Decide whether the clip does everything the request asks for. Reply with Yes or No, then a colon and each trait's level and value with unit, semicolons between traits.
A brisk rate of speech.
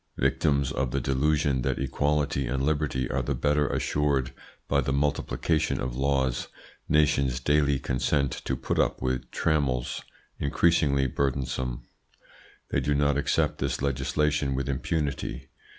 No: slow, 135 wpm